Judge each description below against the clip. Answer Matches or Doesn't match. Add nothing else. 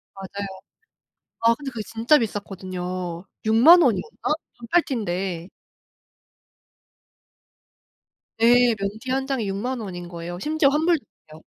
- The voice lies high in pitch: Matches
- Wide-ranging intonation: Matches